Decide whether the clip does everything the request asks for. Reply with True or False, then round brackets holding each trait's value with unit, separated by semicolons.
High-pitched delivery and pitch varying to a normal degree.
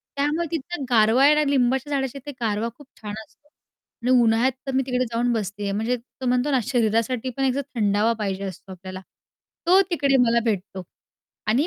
True (245 Hz; 4.1 semitones)